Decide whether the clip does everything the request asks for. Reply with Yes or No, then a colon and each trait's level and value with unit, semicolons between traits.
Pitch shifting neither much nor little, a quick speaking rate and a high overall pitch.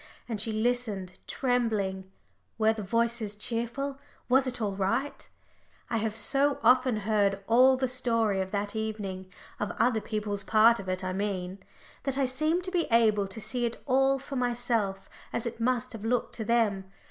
No: average, 3.6 semitones; average, 175 wpm; high, 225 Hz